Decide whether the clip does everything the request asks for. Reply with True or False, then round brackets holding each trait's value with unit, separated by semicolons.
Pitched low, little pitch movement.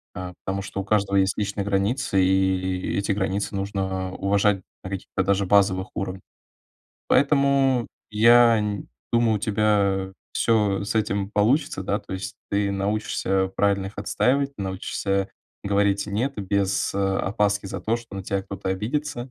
True (100 Hz; 1.8 semitones)